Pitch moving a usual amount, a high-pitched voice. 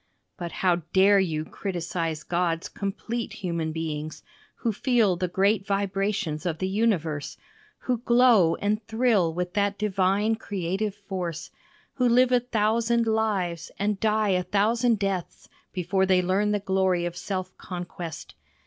Yes: average, 3.4 semitones; high, 195 Hz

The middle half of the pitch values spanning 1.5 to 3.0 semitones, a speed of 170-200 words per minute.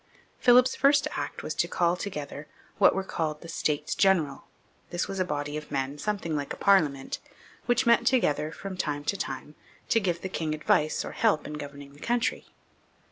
No: average, 5.2 semitones; average, 190 wpm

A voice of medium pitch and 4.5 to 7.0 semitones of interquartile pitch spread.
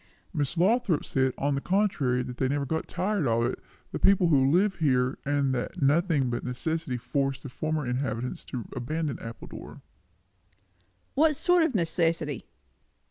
Yes: medium, 145 Hz; average, 4.9 semitones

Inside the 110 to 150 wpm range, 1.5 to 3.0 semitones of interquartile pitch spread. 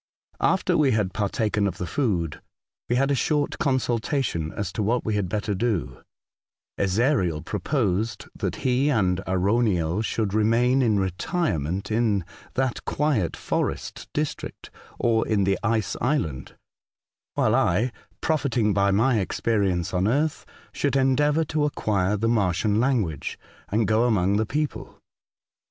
No: average, 140 wpm; average, 5.0 semitones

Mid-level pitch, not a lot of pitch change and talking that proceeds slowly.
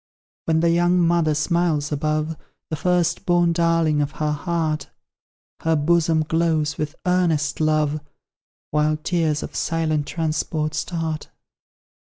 Yes: medium, 160 Hz; narrow, 1.8 semitones; slow, 125 wpm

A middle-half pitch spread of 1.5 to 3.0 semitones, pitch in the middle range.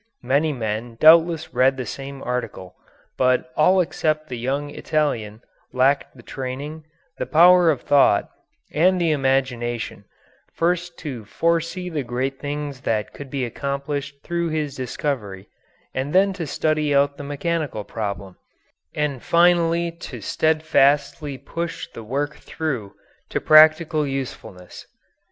No: average, 3.7 semitones; medium, 145 Hz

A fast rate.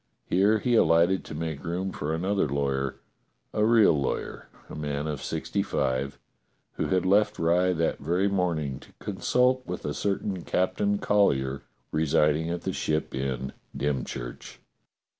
No: average, 145 wpm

